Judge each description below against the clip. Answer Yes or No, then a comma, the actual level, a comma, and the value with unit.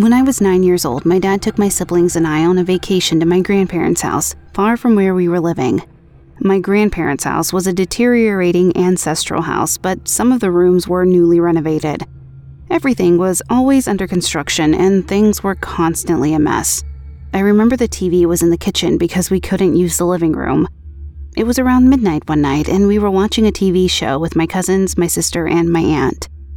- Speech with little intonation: No, average, 3.0 semitones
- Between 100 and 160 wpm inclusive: No, average, 200 wpm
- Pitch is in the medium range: Yes, medium, 180 Hz